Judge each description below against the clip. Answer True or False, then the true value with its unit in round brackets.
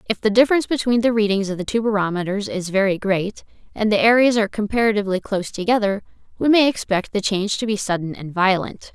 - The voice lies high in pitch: True (210 Hz)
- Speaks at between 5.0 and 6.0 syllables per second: False (6.5 syllables/s)